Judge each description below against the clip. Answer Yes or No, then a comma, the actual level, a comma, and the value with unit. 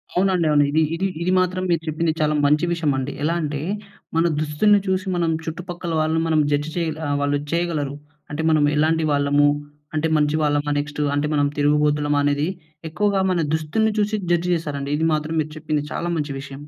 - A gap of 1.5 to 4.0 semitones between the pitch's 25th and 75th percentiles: Yes, narrow, 2.6 semitones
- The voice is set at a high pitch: No, medium, 155 Hz